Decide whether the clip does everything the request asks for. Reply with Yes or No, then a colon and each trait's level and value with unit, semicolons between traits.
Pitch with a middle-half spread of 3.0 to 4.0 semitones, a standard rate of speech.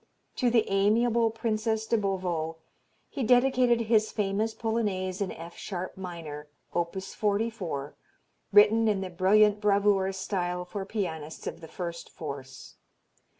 No: average, 3.7 semitones; slow, 130 wpm